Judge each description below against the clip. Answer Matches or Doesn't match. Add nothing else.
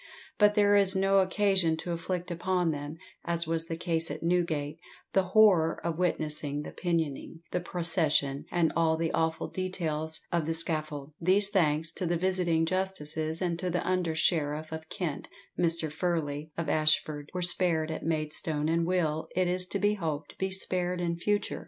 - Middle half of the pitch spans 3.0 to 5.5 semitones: Doesn't match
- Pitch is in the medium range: Matches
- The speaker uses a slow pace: Doesn't match